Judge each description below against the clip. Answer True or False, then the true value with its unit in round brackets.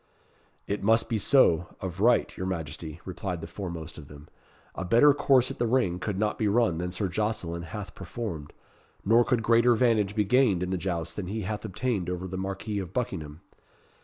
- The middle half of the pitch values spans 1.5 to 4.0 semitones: False (4.4 semitones)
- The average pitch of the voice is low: True (95 Hz)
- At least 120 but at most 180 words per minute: False (195 wpm)